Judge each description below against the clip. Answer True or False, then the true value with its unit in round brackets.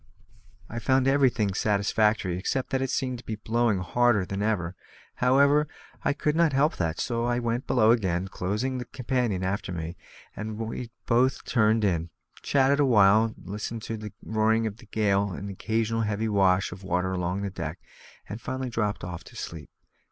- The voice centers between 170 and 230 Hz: False (110 Hz)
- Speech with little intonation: False (3.8 semitones)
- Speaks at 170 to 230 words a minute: True (180 wpm)